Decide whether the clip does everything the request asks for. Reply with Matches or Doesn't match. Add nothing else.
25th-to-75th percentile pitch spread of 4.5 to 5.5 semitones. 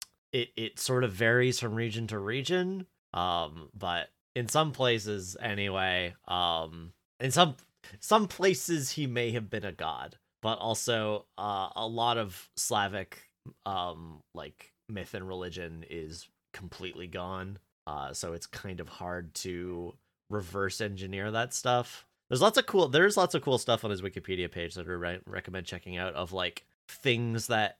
Matches